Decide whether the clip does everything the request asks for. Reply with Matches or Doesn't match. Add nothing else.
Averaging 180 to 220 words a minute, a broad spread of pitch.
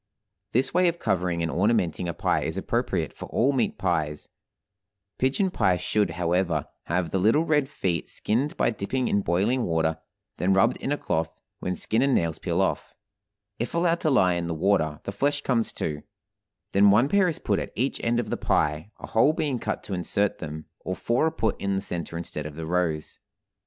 Matches